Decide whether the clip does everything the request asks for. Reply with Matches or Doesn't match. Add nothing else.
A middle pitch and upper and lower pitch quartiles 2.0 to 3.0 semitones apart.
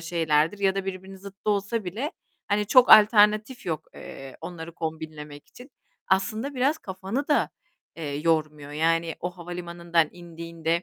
Doesn't match